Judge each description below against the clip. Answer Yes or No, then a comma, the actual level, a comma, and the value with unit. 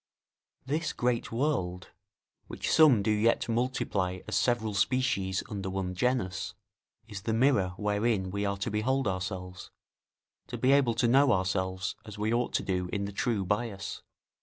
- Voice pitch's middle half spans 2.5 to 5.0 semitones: Yes, average, 4.3 semitones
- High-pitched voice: No, low, 105 Hz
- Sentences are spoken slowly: No, average, 160 wpm